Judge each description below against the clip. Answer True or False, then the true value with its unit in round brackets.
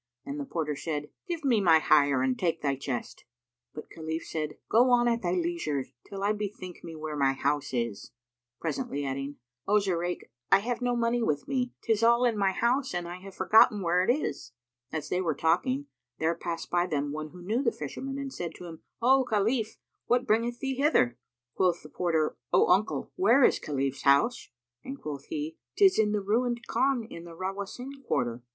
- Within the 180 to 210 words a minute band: True (200 wpm)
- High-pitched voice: False (180 Hz)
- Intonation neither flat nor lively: False (7.6 semitones)